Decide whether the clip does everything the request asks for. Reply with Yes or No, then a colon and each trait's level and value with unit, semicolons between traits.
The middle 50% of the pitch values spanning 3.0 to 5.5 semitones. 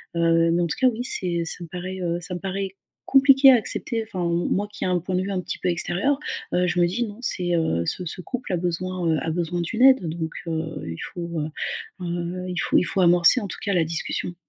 No: narrow, 2.5 semitones